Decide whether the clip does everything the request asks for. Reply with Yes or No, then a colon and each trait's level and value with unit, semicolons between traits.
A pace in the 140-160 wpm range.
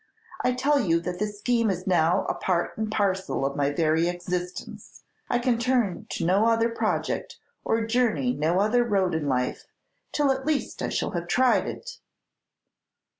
No: average, 175 wpm